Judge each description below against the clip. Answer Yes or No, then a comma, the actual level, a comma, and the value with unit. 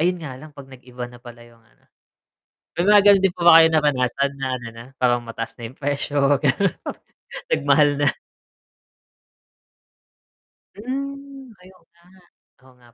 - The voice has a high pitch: No, medium, 145 Hz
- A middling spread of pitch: No, wide, 6.3 semitones